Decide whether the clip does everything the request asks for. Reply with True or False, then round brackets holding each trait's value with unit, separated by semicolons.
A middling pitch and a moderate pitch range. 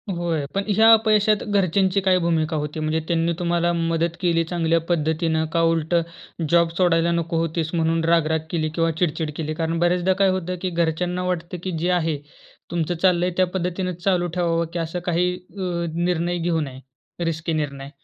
False (170 Hz; 1.6 semitones)